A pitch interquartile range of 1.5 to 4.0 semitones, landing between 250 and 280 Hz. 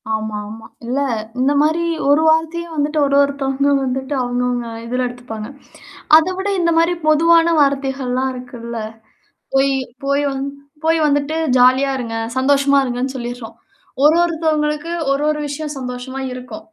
Yes: average, 3.4 semitones; very high, 275 Hz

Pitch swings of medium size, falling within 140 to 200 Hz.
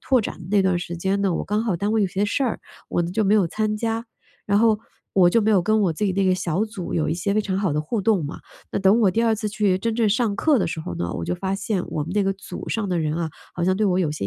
Yes: average, 3.6 semitones; high, 195 Hz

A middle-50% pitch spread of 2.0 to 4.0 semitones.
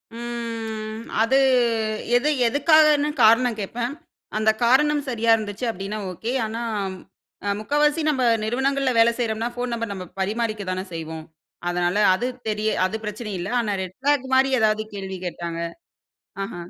Yes: average, 3.6 semitones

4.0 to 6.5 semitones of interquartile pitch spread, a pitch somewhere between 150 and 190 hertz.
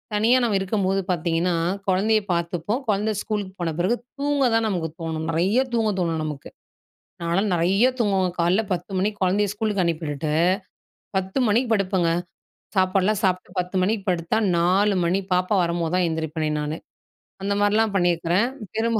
No: average, 3.6 semitones; medium, 185 Hz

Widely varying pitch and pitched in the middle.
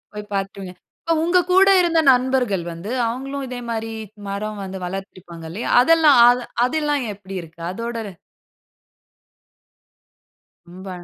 No: wide, 5.8 semitones; high, 225 Hz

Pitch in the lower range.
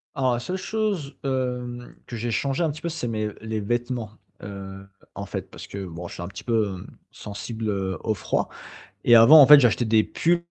Yes: low, 120 Hz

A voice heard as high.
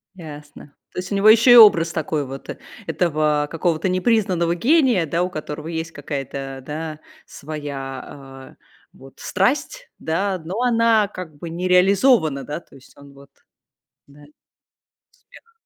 No: medium, 165 Hz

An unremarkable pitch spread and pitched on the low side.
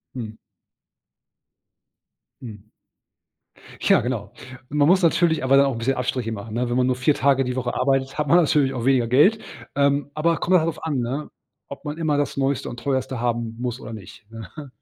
Yes: average, 3.4 semitones; low, 130 Hz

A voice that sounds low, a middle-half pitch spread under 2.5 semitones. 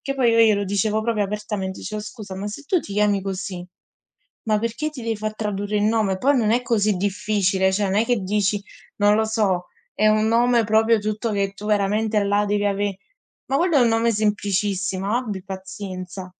No: high, 210 Hz; narrow, 2.0 semitones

